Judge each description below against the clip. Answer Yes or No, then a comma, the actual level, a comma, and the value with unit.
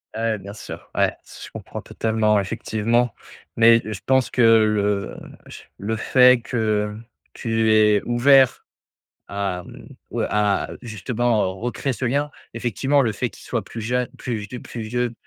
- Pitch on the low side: Yes, low, 115 Hz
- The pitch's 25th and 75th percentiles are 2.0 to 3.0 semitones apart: Yes, narrow, 2.5 semitones